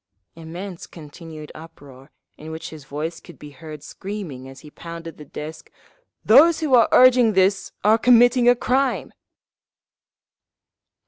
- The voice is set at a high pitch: No, medium, 165 Hz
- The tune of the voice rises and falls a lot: Yes, wide, 7.2 semitones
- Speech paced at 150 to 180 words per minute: No, slow, 135 wpm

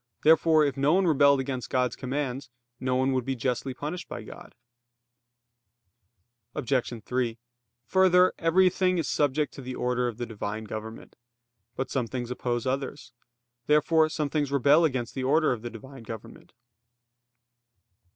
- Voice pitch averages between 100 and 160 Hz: Yes, low, 135 Hz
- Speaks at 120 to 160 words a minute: Yes, average, 150 wpm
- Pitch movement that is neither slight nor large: Yes, average, 3.5 semitones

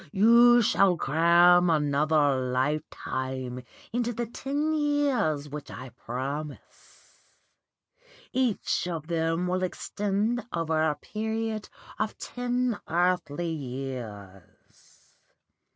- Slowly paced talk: Yes, slow, 90 wpm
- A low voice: No, medium, 170 Hz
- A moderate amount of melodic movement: No, wide, 7.5 semitones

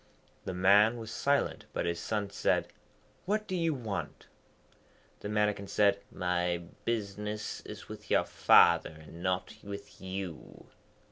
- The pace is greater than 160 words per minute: No, slow, 135 wpm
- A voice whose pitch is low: Yes, low, 100 Hz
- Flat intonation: No, average, 3.0 semitones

